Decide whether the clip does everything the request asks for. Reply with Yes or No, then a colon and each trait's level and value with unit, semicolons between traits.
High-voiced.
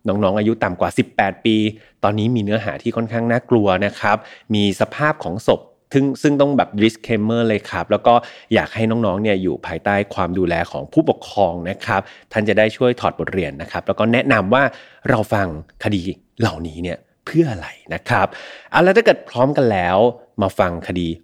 No: low, 105 Hz